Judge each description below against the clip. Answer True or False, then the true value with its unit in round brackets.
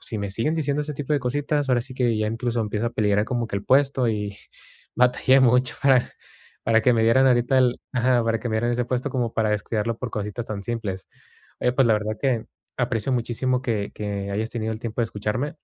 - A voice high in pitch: False (120 Hz)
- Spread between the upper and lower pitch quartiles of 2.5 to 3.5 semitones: True (2.9 semitones)